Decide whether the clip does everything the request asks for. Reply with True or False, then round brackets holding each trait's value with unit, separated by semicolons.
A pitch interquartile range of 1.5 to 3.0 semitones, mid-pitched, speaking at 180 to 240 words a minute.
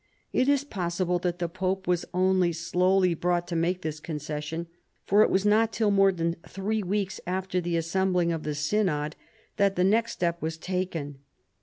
True (2.5 semitones; 180 Hz; 185 wpm)